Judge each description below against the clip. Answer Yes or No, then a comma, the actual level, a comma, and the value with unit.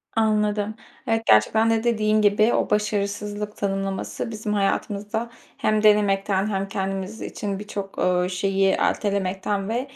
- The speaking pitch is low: No, high, 205 Hz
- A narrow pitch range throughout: Yes, narrow, 1.6 semitones